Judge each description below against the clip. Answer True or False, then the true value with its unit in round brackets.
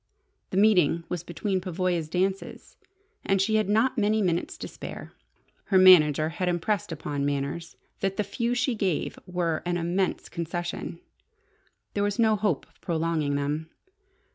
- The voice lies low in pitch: False (180 Hz)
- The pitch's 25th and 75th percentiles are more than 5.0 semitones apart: False (3.6 semitones)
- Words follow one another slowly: False (150 wpm)